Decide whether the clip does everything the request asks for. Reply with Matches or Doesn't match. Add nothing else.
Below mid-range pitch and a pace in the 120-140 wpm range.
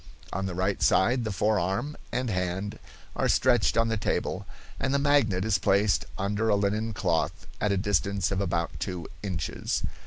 Doesn't match